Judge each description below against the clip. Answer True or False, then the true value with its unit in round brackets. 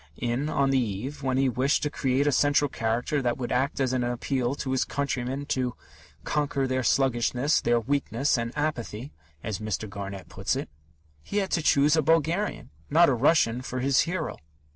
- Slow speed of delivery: False (185 wpm)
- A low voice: True (130 Hz)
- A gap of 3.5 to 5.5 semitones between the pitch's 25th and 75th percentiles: False (3.1 semitones)